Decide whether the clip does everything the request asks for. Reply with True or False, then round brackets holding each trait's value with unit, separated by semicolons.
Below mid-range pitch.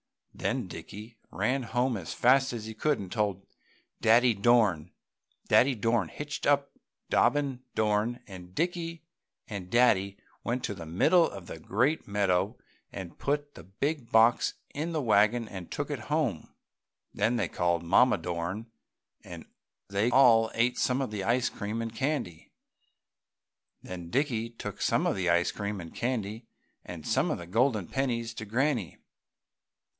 True (115 Hz)